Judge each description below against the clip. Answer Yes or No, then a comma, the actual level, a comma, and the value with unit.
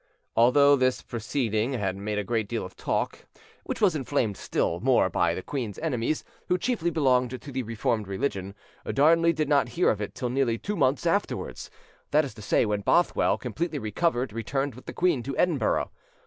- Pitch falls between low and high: No, low, 130 Hz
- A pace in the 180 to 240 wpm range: Yes, average, 185 wpm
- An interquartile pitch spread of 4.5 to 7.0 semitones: Yes, average, 5.1 semitones